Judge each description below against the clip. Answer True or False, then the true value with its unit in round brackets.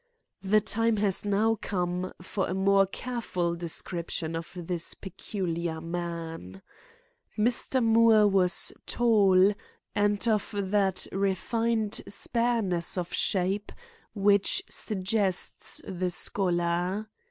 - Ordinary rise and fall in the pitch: True (3.1 semitones)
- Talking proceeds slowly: True (100 wpm)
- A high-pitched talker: True (195 Hz)